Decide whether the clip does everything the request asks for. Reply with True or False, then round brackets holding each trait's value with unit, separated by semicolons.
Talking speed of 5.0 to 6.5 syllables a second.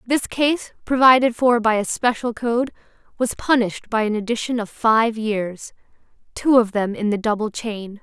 False (4.7 syllables/s)